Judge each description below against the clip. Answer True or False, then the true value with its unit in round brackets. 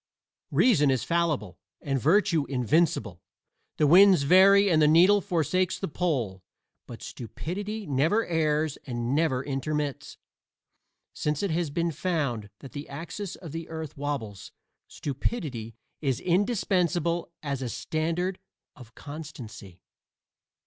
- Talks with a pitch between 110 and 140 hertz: False (155 Hz)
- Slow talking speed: True (120 wpm)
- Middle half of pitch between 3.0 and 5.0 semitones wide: True (4.5 semitones)